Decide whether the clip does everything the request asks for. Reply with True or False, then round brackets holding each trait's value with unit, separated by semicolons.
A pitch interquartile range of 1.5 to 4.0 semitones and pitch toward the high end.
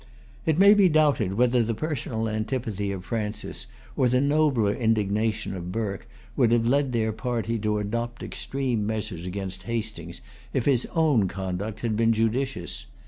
False (3.3 semitones; 115 Hz)